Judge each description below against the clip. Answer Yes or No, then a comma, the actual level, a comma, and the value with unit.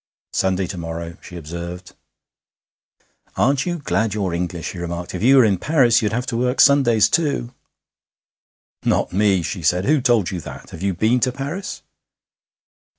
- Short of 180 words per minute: Yes, average, 165 wpm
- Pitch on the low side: Yes, low, 105 Hz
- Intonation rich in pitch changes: Yes, wide, 6.2 semitones